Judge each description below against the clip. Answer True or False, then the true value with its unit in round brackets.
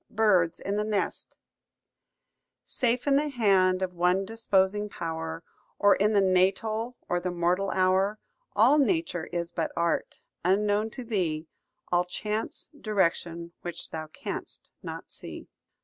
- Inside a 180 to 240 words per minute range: False (135 wpm)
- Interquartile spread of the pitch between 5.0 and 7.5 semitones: False (3.5 semitones)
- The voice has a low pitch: False (190 Hz)